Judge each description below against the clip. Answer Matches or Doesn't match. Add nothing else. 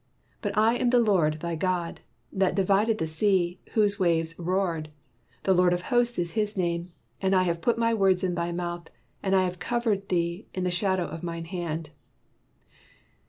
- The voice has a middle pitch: Matches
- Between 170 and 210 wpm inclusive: Matches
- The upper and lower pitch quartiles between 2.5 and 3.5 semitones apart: Matches